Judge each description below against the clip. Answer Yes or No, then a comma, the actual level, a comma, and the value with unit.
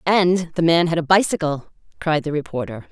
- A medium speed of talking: Yes, average, 185 wpm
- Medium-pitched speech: Yes, medium, 160 Hz